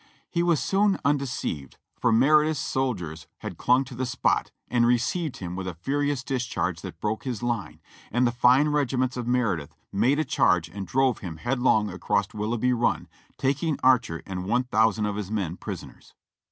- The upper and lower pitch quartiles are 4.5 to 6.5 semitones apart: Yes, average, 4.8 semitones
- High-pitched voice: No, low, 120 Hz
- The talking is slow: No, average, 180 wpm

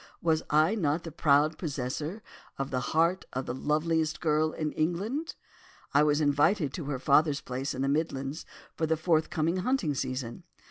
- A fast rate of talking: No, average, 170 wpm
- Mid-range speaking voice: Yes, medium, 155 Hz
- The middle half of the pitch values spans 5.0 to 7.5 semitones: No, average, 2.8 semitones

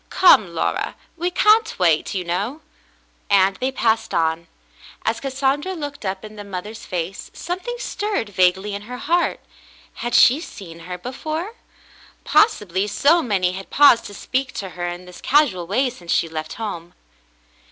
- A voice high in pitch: Yes, high, 210 Hz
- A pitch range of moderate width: No, wide, 7.8 semitones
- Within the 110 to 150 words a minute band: No, average, 160 wpm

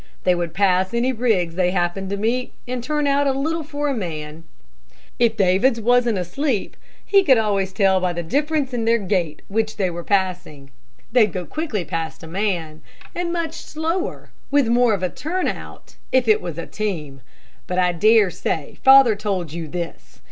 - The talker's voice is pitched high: Yes, high, 205 Hz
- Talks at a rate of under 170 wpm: No, average, 185 wpm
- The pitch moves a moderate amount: No, wide, 6.3 semitones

